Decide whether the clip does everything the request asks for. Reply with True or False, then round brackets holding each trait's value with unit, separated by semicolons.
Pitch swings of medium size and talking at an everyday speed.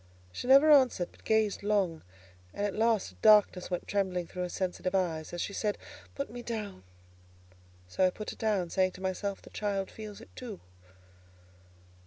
True (3.1 semitones; 180 wpm)